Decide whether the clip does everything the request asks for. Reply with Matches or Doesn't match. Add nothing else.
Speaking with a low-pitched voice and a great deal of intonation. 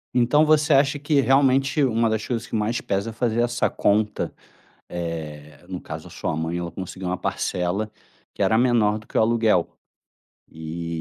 Matches